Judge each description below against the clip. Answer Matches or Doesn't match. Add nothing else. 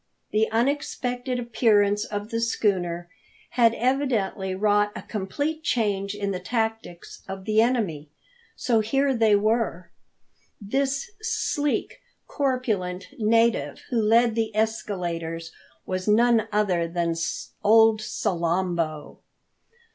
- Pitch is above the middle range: Matches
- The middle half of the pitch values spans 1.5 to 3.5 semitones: Doesn't match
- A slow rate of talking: Matches